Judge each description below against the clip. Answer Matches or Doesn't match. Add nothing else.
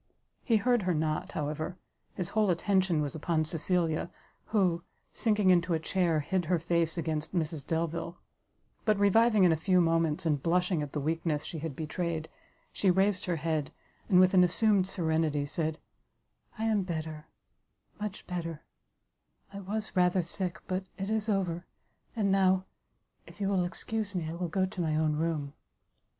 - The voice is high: Doesn't match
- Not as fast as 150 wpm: Doesn't match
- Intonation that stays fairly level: Doesn't match